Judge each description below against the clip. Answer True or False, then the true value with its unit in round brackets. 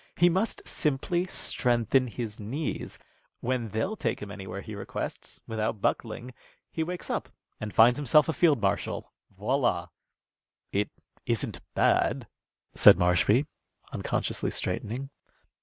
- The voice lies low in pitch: True (120 Hz)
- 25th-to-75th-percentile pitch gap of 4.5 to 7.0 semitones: True (5.6 semitones)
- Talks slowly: True (125 wpm)